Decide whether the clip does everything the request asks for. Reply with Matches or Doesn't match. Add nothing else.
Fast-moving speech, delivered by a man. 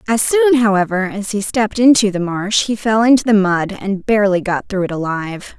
Doesn't match